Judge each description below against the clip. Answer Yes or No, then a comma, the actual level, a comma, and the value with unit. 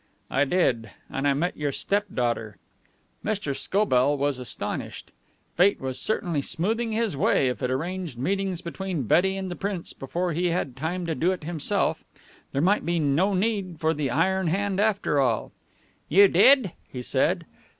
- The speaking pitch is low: No, medium, 170 Hz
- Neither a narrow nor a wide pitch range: No, wide, 5.7 semitones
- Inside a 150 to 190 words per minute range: Yes, average, 165 wpm